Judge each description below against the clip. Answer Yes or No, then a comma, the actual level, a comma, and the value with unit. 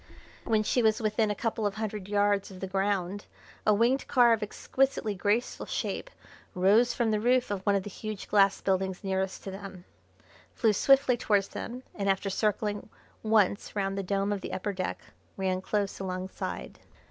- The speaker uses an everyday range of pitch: No, narrow, 2.2 semitones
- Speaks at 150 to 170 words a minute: No, average, 180 wpm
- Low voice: No, high, 205 Hz